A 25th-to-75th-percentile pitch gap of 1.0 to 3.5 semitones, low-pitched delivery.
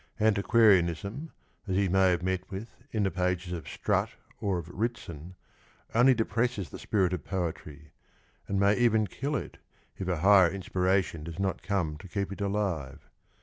Yes: average, 2.9 semitones; very low, 95 Hz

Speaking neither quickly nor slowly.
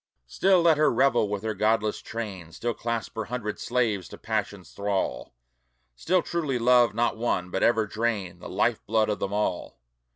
Yes: average, 175 wpm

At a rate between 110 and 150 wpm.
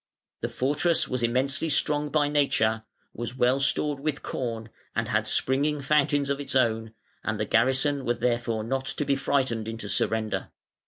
No: average, 165 wpm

